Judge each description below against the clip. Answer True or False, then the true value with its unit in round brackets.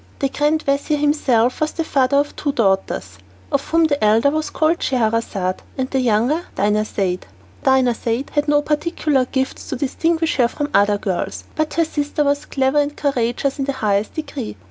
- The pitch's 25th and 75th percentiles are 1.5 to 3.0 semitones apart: False (4.5 semitones)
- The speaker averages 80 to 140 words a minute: False (175 wpm)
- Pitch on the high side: True (270 Hz)